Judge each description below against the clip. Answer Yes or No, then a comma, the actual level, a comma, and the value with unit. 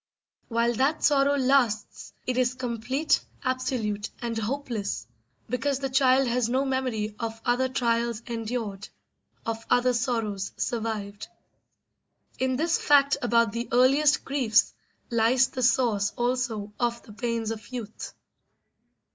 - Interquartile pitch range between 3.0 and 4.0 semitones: No, narrow, 2.5 semitones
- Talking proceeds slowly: Yes, slow, 125 wpm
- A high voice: Yes, high, 240 Hz